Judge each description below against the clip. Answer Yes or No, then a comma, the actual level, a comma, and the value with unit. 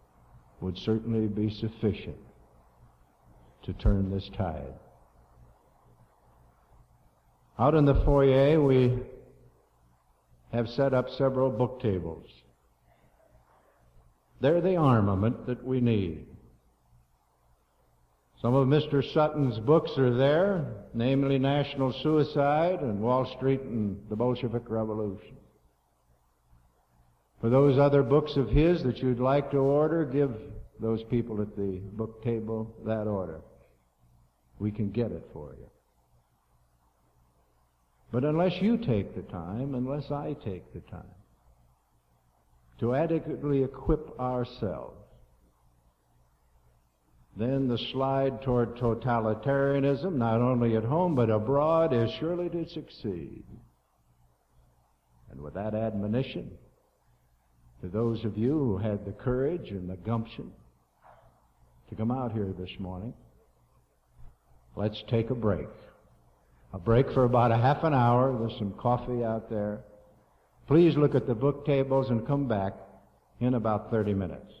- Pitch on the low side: Yes, low, 110 Hz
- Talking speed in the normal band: No, slow, 120 wpm